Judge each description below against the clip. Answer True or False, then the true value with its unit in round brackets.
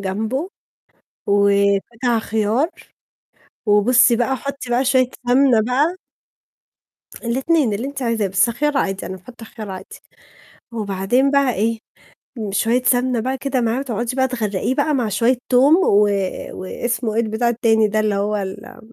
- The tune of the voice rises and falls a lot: False (3.6 semitones)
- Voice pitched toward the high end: True (235 Hz)